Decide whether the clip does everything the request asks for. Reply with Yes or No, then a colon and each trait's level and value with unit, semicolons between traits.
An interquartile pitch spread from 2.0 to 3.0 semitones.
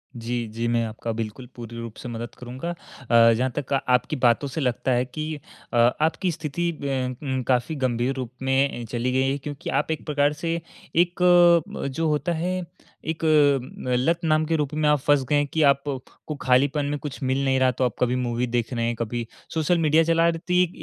No: average, 4.0 semitones